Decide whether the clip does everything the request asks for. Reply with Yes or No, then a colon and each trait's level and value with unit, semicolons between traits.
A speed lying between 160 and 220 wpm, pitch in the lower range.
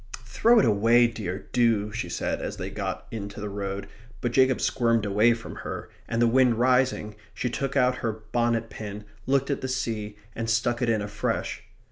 Yes: average, 190 wpm; low, 115 Hz